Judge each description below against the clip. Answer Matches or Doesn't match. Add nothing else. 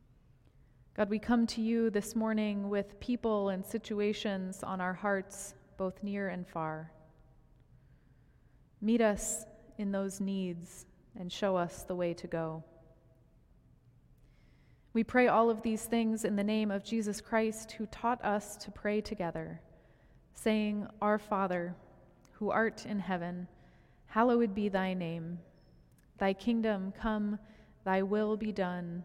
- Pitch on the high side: Matches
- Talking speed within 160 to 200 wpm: Doesn't match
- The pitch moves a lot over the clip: Doesn't match